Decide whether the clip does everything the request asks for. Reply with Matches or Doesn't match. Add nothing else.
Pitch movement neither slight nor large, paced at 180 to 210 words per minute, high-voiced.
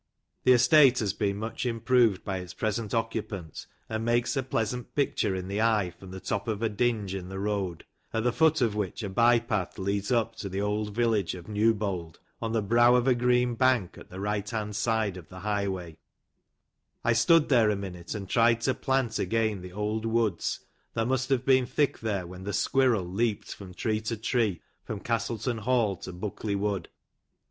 Doesn't match